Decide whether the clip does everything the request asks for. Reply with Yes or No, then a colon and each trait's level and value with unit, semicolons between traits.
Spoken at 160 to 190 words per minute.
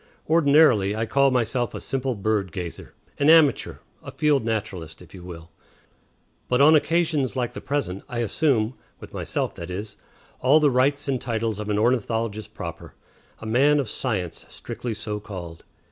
Yes: average, 165 wpm